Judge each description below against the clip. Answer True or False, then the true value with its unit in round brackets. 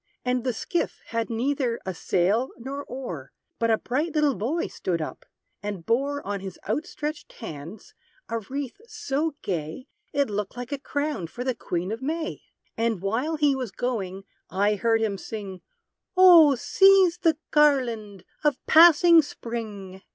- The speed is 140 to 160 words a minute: True (155 wpm)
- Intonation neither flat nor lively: False (6.2 semitones)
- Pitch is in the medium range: False (240 Hz)